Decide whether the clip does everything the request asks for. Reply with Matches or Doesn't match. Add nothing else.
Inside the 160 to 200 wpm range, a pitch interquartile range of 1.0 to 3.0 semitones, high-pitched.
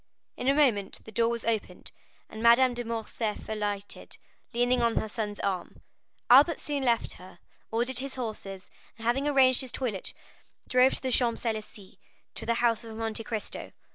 Matches